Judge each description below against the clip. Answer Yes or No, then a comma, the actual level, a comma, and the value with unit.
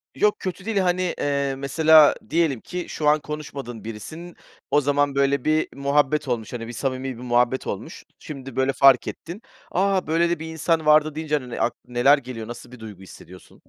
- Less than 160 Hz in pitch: Yes, medium, 140 Hz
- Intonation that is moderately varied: Yes, average, 4.1 semitones